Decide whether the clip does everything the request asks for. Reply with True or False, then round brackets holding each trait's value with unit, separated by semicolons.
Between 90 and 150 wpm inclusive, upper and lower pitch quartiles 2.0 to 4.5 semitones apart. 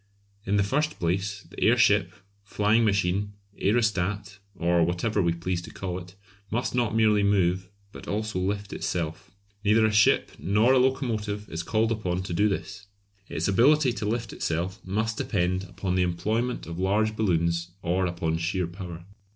False (165 wpm; 3.5 semitones)